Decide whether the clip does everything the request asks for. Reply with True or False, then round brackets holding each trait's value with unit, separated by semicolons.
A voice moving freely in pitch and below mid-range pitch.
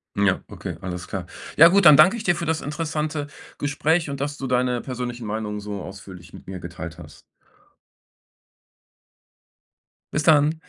True (8.0 semitones; 125 Hz)